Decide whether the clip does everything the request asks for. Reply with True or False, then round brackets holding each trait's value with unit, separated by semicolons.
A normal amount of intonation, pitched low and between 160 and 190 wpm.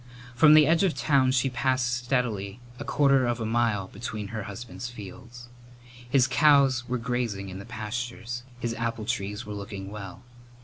True (3.3 semitones; 120 Hz; 170 wpm)